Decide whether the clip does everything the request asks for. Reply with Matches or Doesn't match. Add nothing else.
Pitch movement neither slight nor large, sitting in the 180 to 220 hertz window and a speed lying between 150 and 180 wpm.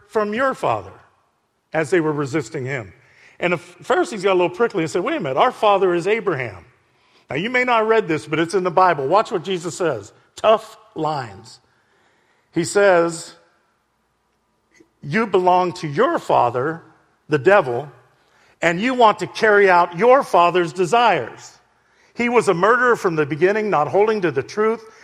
Matches